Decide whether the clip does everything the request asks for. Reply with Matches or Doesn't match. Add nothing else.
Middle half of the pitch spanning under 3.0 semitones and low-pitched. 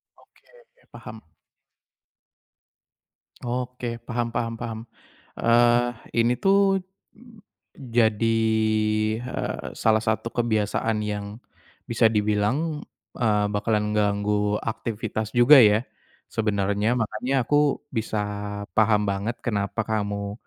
Matches